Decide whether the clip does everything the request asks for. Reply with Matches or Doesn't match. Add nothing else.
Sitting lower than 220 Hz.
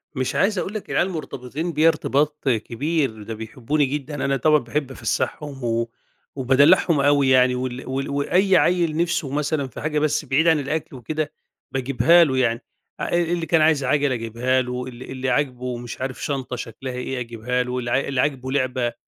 Matches